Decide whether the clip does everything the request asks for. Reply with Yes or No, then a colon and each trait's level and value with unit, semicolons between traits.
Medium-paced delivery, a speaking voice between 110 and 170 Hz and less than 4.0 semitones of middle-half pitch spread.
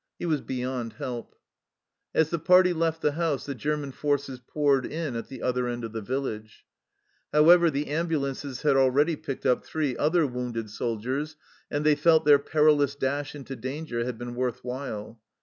Yes: average, 175 wpm; medium, 140 Hz; average, 3.5 semitones